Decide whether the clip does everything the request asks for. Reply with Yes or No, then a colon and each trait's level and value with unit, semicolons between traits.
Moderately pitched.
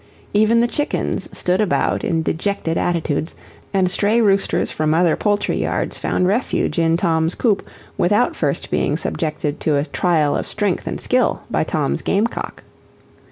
Yes: medium, 180 Hz